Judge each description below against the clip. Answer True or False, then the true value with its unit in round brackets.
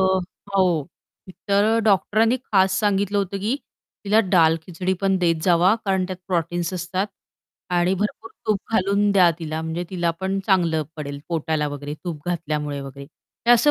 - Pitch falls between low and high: True (180 Hz)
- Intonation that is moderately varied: True (3.5 semitones)